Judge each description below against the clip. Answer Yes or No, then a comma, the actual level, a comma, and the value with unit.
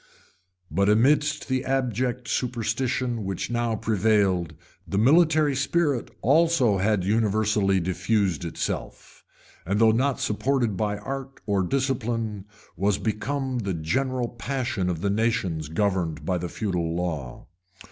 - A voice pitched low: Yes, low, 110 Hz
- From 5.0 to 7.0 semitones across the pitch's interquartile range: Yes, average, 5.3 semitones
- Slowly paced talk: Yes, slow, 125 wpm